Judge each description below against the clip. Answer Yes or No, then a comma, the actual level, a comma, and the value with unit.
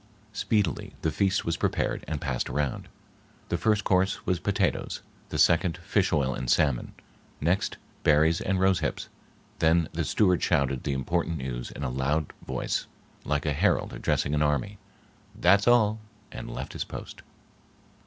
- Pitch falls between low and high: No, very low, 80 Hz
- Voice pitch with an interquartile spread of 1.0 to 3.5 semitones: No, average, 5.1 semitones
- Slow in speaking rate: No, average, 155 wpm